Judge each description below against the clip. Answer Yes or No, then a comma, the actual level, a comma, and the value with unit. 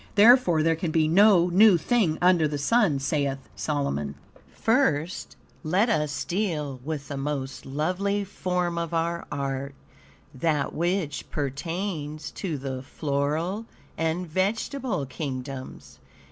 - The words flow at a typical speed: No, slow, 120 wpm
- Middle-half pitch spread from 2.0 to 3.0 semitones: No, average, 4.5 semitones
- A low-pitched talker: No, medium, 160 Hz